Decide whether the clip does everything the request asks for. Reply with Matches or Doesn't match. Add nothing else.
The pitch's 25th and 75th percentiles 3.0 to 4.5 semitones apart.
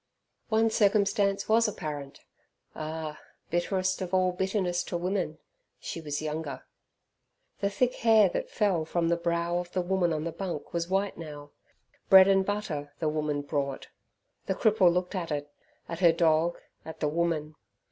Matches